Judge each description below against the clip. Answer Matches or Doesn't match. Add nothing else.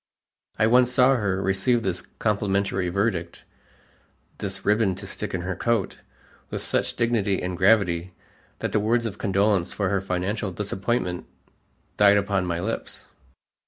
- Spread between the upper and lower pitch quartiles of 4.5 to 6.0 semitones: Doesn't match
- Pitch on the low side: Matches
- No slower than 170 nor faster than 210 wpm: Doesn't match